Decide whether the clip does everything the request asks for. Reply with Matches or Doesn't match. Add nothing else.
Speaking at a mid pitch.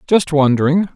Matches